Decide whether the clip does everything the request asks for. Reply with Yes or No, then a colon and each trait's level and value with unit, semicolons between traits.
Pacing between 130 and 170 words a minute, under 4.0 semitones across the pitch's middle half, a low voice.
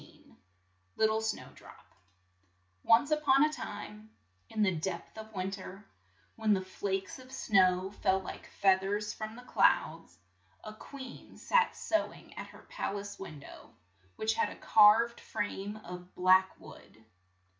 No: average, 150 wpm; average, 2.7 semitones; high, 205 Hz